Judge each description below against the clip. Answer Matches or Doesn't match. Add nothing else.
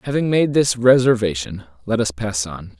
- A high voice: Doesn't match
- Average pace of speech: Matches